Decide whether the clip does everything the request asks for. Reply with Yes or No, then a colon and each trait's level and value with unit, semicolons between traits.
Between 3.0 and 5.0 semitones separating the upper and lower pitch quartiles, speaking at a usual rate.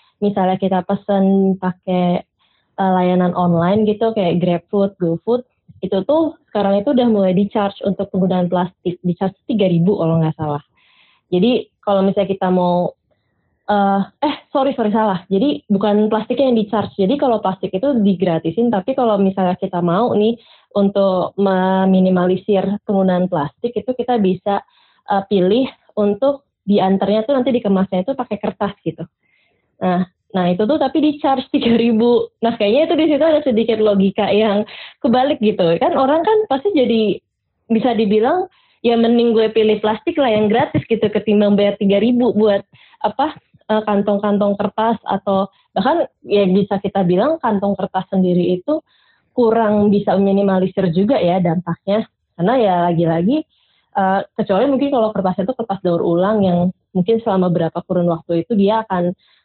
No: average, 3.6 semitones; fast, 150 wpm